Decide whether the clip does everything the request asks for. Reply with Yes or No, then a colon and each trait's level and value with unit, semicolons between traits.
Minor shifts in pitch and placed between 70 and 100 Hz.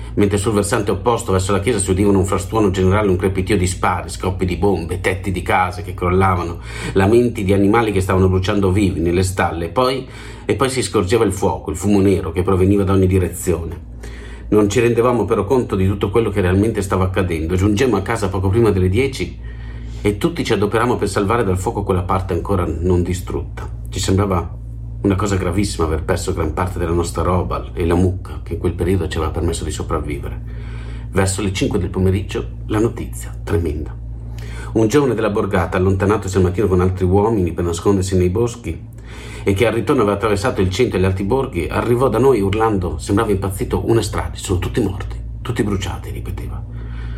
No: average, 3.0 semitones; very low, 95 Hz